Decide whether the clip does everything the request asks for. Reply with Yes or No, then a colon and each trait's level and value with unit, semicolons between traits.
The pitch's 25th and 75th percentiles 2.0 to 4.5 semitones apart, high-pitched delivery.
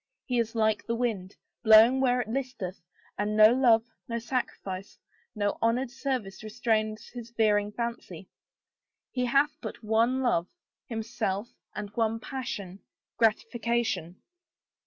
Yes: narrow, 2.5 semitones; high, 225 Hz